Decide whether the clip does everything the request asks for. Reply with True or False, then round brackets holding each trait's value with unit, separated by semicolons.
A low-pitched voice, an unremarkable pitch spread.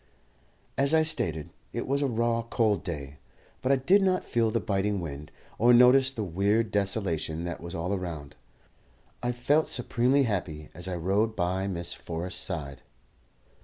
False (100 Hz; 6.1 semitones)